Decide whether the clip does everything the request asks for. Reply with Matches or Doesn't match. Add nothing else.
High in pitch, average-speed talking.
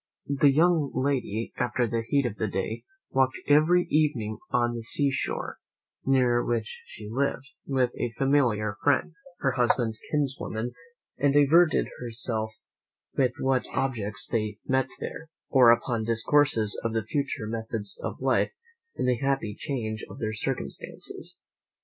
Doesn't match